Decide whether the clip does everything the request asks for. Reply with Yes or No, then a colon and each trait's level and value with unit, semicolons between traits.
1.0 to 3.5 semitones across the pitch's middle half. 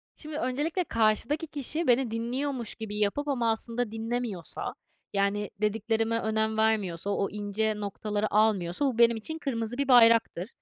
Yes: average, 3.0 semitones